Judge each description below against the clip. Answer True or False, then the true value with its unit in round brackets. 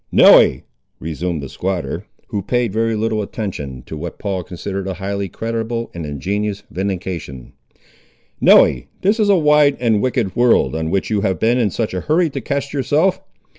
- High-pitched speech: False (105 Hz)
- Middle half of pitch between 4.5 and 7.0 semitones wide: True (5.1 semitones)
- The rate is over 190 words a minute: False (175 wpm)